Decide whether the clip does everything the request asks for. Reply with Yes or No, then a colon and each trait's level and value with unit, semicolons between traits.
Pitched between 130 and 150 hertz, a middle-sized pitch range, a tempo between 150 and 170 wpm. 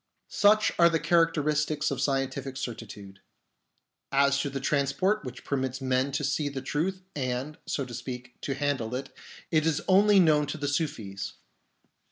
Yes: medium, 140 Hz; average, 3.0 semitones; average, 165 wpm